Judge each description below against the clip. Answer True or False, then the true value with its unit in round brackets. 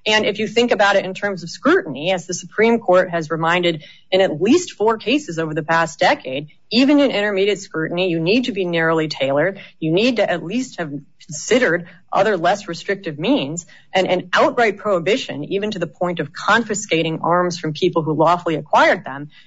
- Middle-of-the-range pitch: True (180 Hz)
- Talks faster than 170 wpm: True (195 wpm)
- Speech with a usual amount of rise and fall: True (3.9 semitones)